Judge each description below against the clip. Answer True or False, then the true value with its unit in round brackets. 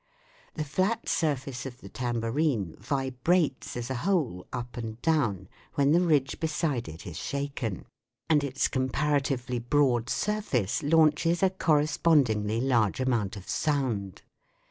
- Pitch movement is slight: False (4.6 semitones)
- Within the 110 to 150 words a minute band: True (145 wpm)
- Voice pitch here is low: True (130 Hz)